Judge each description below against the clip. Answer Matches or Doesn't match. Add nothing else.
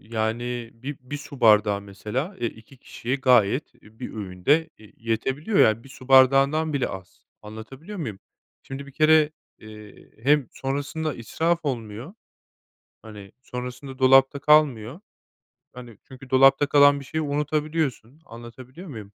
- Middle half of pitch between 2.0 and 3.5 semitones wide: Doesn't match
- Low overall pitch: Matches